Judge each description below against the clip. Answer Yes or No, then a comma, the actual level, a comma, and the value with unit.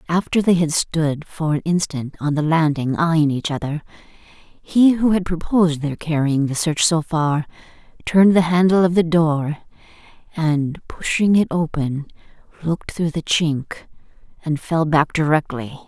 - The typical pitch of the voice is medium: Yes, medium, 160 Hz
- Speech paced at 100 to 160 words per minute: Yes, average, 155 wpm